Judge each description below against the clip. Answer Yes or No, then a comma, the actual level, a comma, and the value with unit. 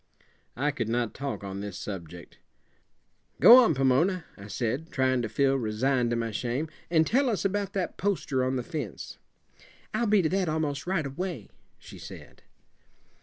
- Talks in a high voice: No, medium, 140 Hz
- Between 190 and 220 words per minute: No, average, 170 wpm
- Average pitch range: No, wide, 7.0 semitones